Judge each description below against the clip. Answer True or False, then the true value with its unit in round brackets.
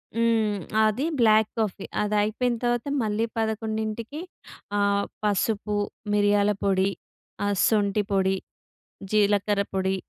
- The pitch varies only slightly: True (1.5 semitones)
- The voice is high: True (210 Hz)